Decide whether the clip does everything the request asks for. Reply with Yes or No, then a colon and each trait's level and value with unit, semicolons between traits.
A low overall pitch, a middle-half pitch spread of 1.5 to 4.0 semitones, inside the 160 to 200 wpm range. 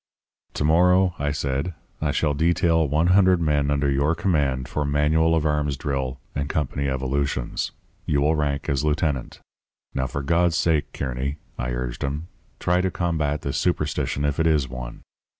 Yes: very low, 75 Hz; average, 2.8 semitones; average, 170 wpm